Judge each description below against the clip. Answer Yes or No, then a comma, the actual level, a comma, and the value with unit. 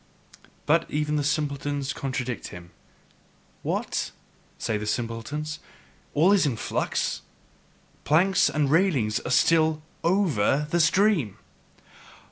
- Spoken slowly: Yes, slow, 100 wpm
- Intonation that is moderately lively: Yes, average, 4.4 semitones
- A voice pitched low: No, medium, 150 Hz